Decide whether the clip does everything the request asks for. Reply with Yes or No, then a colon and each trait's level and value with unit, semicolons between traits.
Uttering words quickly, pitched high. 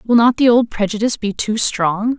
Yes: fast, 220 wpm; high, 220 Hz